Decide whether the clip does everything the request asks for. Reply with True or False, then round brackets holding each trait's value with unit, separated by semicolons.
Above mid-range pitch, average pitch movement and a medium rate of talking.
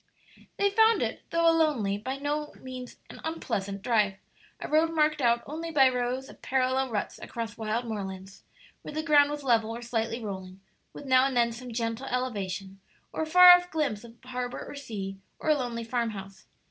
True (250 Hz; 5.0 semitones; 190 wpm)